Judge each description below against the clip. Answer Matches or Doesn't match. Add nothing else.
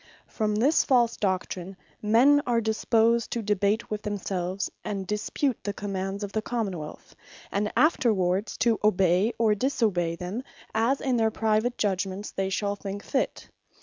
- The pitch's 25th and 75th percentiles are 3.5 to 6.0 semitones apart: Doesn't match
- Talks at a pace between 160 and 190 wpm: Doesn't match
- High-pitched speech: Matches